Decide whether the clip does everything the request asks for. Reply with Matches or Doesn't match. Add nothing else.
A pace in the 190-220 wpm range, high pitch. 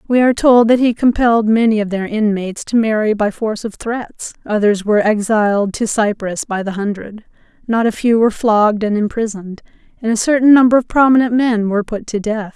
Matches